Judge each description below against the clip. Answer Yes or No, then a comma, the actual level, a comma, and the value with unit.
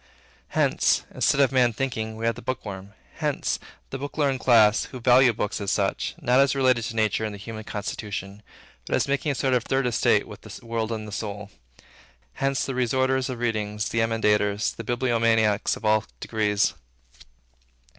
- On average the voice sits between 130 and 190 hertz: No, low, 115 Hz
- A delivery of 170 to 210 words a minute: Yes, average, 180 wpm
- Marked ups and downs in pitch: No, average, 3.5 semitones